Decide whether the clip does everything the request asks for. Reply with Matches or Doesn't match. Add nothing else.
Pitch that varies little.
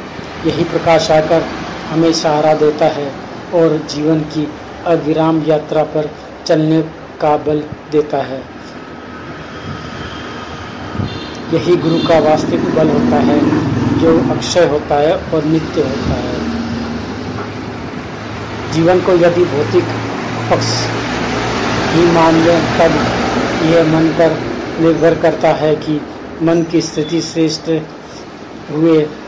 Matches